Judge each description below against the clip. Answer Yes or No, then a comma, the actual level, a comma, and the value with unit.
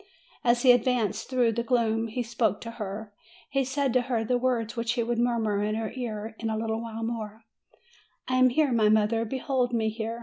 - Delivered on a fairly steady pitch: Yes, narrow, 1.9 semitones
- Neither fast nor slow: No, fast, 215 wpm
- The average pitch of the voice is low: No, high, 230 Hz